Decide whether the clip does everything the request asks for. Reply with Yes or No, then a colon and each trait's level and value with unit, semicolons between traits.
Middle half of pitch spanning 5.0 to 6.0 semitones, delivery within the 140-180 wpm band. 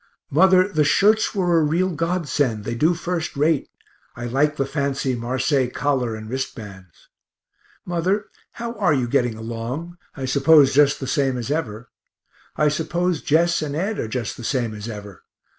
Yes: wide, 5.5 semitones; average, 170 wpm